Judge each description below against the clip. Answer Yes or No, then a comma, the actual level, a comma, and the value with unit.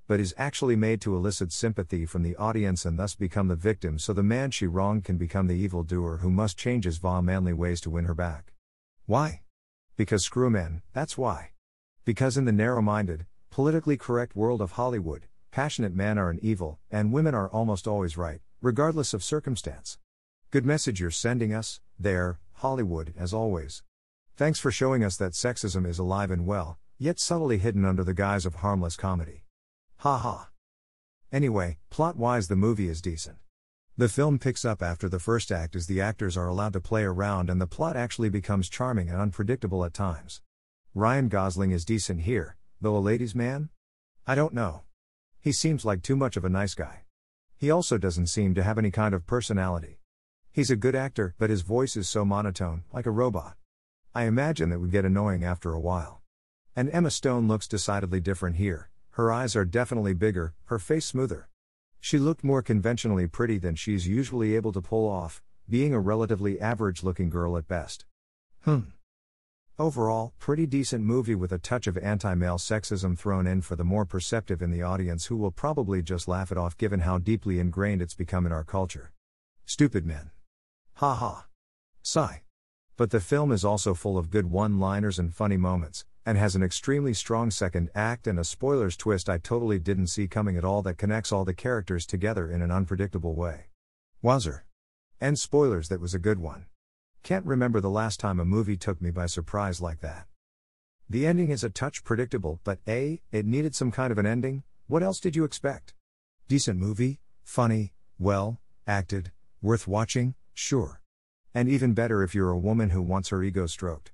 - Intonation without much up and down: No, average, 4.7 semitones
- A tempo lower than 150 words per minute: No, average, 190 wpm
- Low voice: Yes, low, 100 Hz